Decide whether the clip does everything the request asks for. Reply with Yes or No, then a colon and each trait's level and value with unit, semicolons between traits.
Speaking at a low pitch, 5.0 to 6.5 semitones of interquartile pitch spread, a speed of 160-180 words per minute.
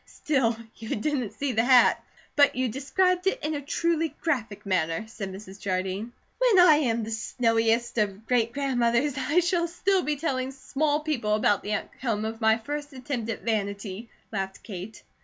No: high, 240 Hz; average, 5.3 semitones; average, 175 wpm